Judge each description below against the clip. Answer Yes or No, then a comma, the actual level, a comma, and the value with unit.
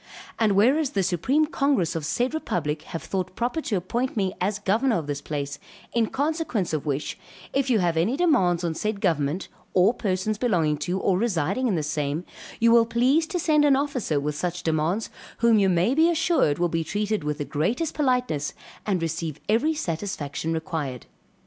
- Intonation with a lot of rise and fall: Yes, wide, 7.4 semitones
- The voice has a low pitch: No, high, 190 Hz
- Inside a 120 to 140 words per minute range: No, average, 185 wpm